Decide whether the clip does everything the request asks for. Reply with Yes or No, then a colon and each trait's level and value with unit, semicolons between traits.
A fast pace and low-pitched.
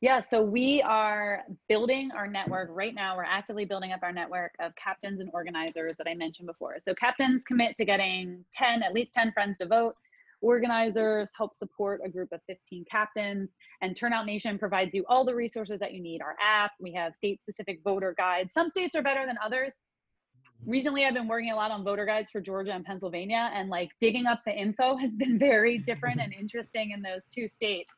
No: fast, 210 wpm; high, 210 Hz